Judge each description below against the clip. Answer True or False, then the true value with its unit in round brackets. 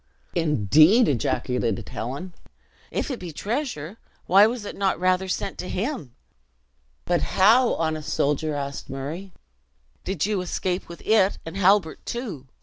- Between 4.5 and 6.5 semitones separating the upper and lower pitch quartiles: True (5.4 semitones)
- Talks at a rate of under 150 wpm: True (140 wpm)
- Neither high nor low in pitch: True (180 Hz)